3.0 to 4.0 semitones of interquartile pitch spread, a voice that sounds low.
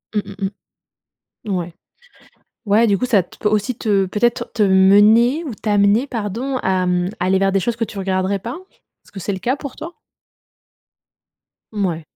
No: average, 3.5 semitones; high, 205 Hz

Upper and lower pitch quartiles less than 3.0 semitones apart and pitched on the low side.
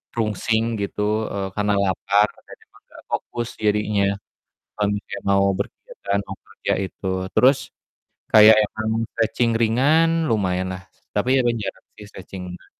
Yes: narrow, 2.5 semitones; low, 105 Hz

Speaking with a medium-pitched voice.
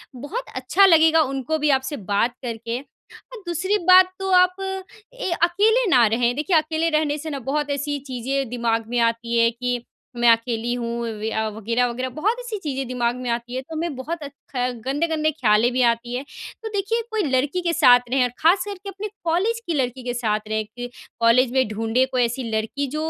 No: very high, 260 Hz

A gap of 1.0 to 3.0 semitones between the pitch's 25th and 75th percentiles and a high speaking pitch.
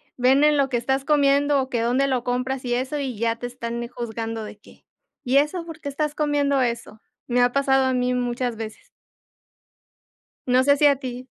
Yes: narrow, 2.5 semitones; very high, 255 Hz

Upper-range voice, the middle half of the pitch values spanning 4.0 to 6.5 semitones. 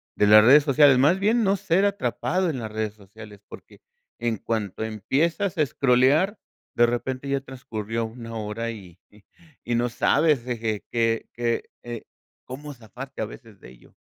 No: low, 120 Hz; average, 4.3 semitones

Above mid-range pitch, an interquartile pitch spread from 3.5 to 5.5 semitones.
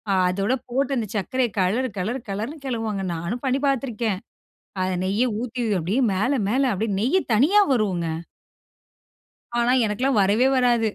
Yes: high, 230 Hz; average, 4.6 semitones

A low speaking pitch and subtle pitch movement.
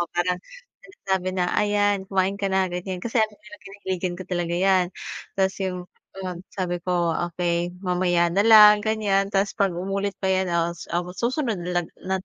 No: high, 190 Hz; narrow, 2.2 semitones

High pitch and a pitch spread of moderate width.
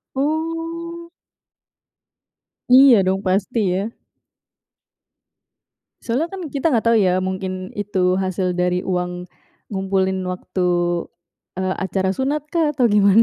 No: high, 195 Hz; wide, 6.6 semitones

